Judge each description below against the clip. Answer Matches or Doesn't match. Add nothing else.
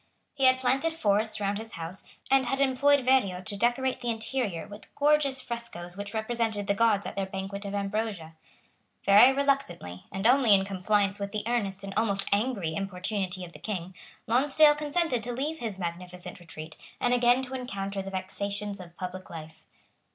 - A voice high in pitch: Matches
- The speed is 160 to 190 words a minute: Matches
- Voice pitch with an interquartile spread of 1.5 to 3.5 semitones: Doesn't match